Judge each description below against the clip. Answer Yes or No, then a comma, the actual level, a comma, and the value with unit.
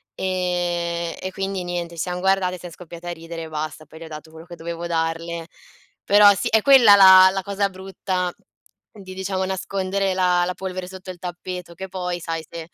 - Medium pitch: Yes, medium, 180 Hz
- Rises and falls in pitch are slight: Yes, narrow, 1.9 semitones